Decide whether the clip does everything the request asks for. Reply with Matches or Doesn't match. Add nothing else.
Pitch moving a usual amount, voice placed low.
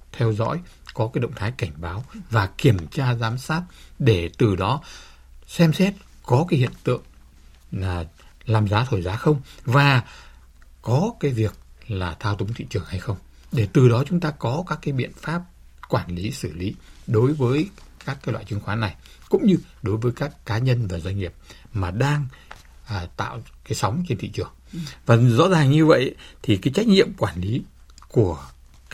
Doesn't match